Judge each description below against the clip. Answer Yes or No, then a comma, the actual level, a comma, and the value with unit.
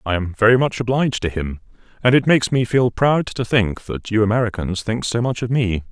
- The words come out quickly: Yes, fast, 235 wpm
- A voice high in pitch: No, low, 115 Hz